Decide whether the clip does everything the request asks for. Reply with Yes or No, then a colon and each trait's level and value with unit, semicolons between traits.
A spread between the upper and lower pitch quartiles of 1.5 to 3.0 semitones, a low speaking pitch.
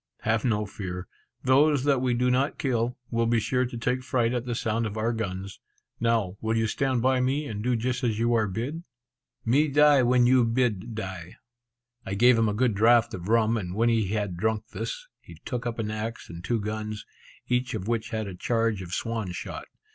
Yes: average, 2.7 semitones; low, 115 Hz